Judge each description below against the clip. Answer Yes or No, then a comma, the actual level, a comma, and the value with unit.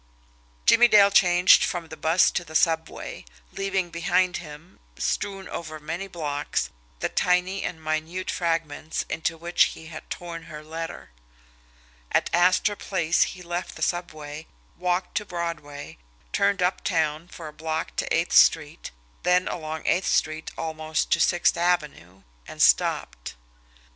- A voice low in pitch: No, medium, 170 Hz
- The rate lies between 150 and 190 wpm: No, average, 140 wpm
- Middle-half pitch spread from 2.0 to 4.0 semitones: Yes, narrow, 2.4 semitones